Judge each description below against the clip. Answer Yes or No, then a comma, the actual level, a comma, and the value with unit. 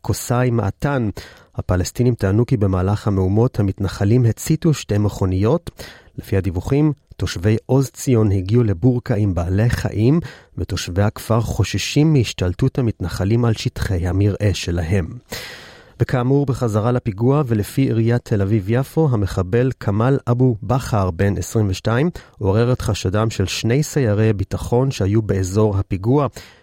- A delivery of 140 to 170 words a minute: No, average, 120 wpm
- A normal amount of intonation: Yes, average, 4.1 semitones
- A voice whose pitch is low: Yes, low, 110 Hz